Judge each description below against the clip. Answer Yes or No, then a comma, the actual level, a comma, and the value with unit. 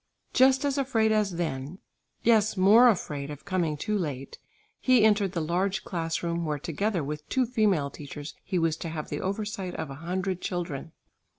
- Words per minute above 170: Yes, average, 180 wpm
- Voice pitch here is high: No, medium, 180 Hz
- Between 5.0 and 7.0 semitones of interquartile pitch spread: Yes, wide, 5.5 semitones